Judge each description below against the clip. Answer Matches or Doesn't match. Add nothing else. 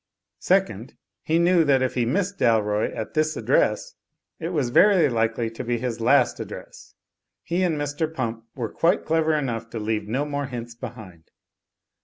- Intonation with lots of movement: Matches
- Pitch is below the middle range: Matches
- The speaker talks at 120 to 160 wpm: Doesn't match